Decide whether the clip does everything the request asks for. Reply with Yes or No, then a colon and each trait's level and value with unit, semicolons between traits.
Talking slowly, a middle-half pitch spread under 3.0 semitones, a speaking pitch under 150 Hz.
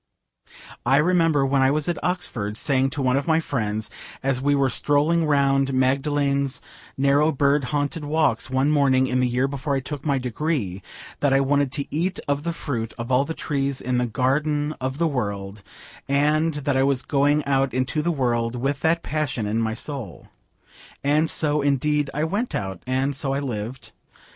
No: average, 185 wpm; narrow, 2.4 semitones; medium, 140 Hz